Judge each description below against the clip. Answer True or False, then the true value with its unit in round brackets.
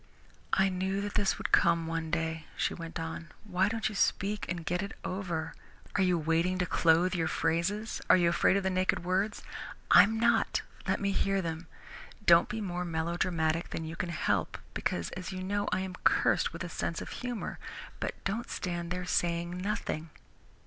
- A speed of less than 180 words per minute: False (190 wpm)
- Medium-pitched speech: True (180 Hz)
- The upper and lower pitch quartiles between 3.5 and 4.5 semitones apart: False (2.7 semitones)